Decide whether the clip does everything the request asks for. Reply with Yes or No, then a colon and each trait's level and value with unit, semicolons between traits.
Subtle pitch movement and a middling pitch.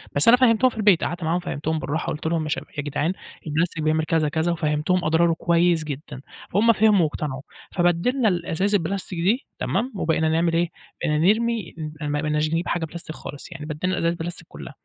No: average, 3.0 semitones; medium, 165 Hz